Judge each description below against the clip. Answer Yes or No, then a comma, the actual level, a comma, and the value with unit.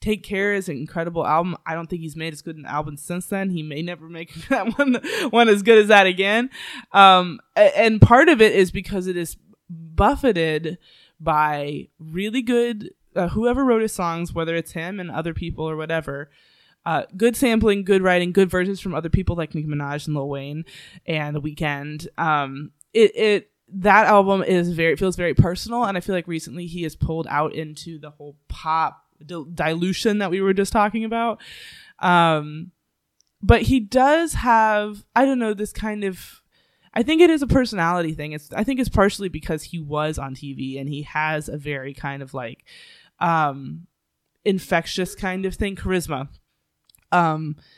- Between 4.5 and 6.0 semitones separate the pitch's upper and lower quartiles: Yes, average, 4.9 semitones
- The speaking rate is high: No, average, 185 wpm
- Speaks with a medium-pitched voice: Yes, medium, 175 Hz